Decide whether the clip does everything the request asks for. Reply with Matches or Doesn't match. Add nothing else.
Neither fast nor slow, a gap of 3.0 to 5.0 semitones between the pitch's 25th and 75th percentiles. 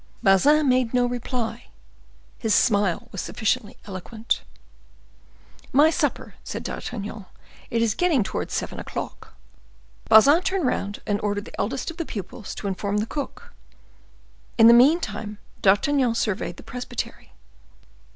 Doesn't match